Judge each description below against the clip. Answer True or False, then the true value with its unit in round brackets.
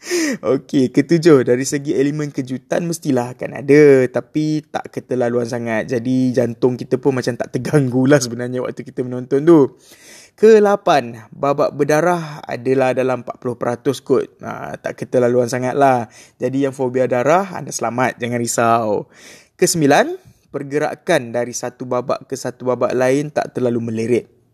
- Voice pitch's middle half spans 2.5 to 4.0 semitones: True (2.9 semitones)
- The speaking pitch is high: False (130 Hz)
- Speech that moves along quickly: False (140 wpm)